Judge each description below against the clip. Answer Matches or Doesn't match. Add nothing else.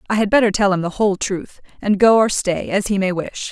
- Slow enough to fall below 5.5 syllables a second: Doesn't match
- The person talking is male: Doesn't match